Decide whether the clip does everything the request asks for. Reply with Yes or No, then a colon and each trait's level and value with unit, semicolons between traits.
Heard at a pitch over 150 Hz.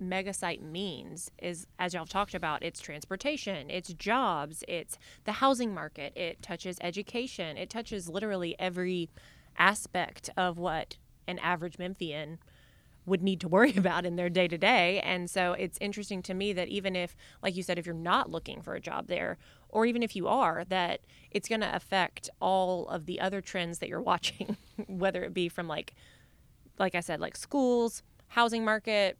Yes: medium, 185 Hz